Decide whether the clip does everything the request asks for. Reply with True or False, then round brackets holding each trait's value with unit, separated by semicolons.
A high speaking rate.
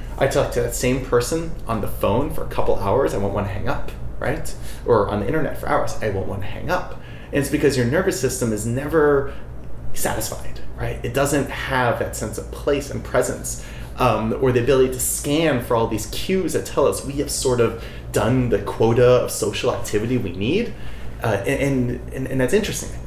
True (215 wpm)